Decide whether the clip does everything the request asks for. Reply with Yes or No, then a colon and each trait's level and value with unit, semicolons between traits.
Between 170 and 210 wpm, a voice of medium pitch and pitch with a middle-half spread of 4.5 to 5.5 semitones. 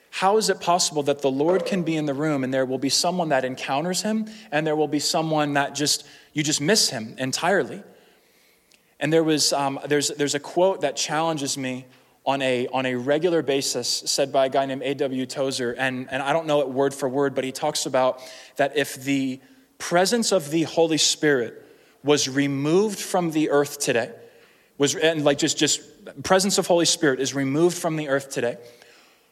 No: average, 200 wpm; medium, 145 Hz; average, 3.2 semitones